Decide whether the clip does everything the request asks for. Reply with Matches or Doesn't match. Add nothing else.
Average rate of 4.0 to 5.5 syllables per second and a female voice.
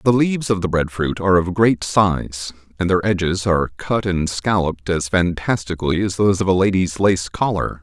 Doesn't match